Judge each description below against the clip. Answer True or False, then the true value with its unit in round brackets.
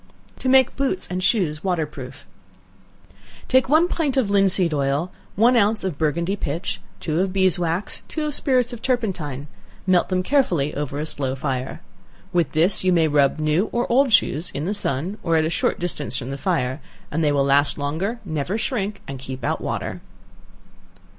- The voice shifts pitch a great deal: True (6.3 semitones)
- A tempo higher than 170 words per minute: True (185 wpm)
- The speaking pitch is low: False (175 Hz)